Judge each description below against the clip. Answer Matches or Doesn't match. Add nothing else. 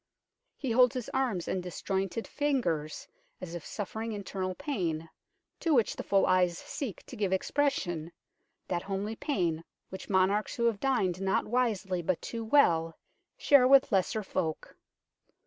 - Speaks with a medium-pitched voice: Doesn't match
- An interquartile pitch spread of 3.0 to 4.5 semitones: Doesn't match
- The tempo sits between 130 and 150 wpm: Matches